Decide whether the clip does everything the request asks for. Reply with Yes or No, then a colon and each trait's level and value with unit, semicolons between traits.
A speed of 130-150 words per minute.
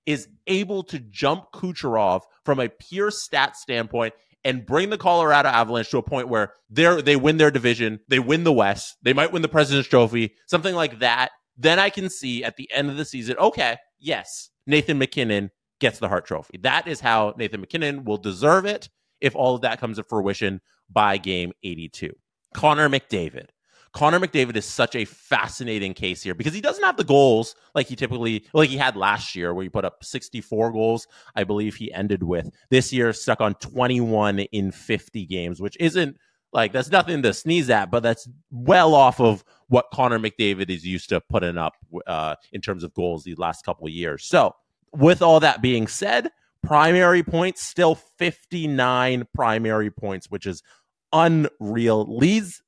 No: average, 185 wpm